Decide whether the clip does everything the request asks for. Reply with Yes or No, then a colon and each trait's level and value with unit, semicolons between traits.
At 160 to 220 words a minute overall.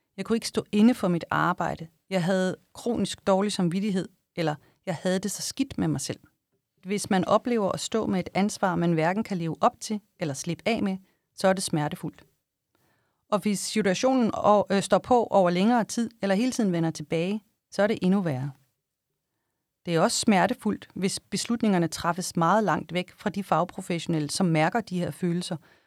Yes: average, 185 wpm